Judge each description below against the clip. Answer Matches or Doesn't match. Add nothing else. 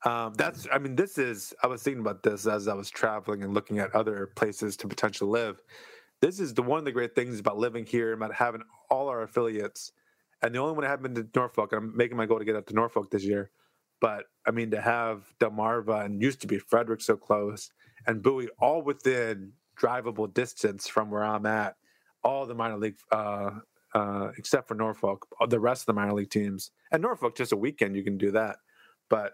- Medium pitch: Doesn't match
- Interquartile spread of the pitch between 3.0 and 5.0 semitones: Doesn't match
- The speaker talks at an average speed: Doesn't match